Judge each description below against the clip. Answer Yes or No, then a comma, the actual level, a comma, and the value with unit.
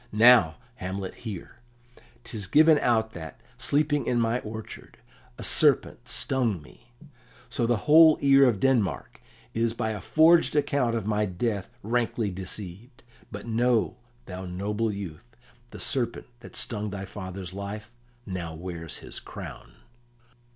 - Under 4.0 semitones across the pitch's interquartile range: No, average, 4.3 semitones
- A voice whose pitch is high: No, low, 110 Hz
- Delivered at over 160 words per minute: No, slow, 135 wpm